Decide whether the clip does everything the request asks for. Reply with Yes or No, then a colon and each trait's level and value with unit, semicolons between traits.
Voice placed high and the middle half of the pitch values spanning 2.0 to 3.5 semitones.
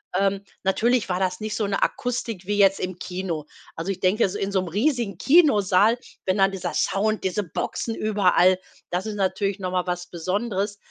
Yes: high, 195 Hz; narrow, 2.5 semitones